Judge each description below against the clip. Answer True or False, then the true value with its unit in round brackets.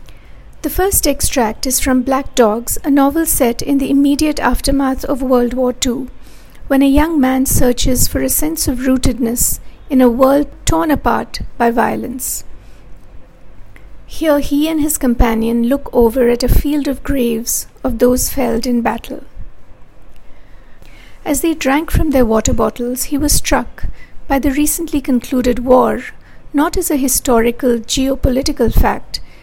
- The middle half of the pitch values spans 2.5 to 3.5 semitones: True (2.8 semitones)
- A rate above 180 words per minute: False (150 wpm)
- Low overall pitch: False (265 Hz)